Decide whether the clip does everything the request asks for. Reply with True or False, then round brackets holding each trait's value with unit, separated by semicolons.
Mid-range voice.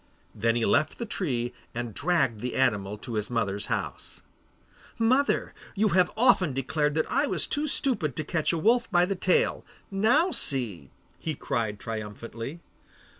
True (150 Hz)